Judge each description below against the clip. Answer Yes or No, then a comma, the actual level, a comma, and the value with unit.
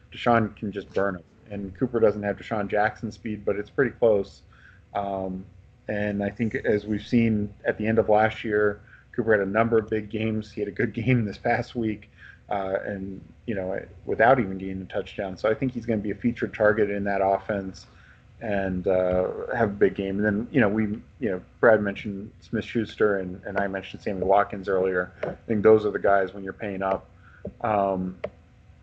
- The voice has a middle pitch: No, low, 105 Hz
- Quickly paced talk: Yes, fast, 210 wpm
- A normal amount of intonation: No, narrow, 2.2 semitones